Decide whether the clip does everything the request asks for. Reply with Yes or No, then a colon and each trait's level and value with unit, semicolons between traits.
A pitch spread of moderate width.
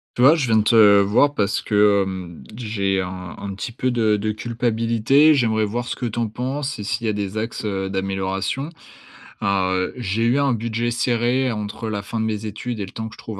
Yes: average, 3.0 semitones